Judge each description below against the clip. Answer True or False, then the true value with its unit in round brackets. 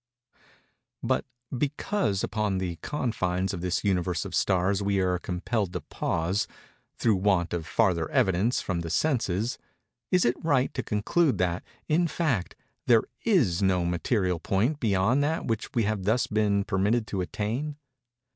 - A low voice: True (100 Hz)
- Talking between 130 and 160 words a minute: True (150 wpm)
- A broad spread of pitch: False (4.8 semitones)